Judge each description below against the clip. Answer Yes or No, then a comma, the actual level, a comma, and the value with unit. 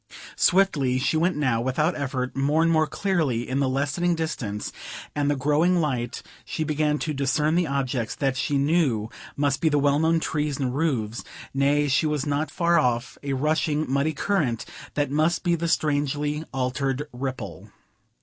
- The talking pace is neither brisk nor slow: Yes, average, 170 wpm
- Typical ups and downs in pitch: Yes, average, 3.1 semitones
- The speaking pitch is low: No, medium, 145 Hz